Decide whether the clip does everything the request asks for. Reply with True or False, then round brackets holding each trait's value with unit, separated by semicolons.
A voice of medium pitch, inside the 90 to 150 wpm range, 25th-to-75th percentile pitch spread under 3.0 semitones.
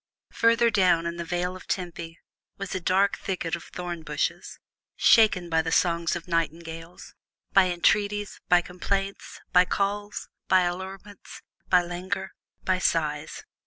True (180 Hz; 140 wpm; 2.5 semitones)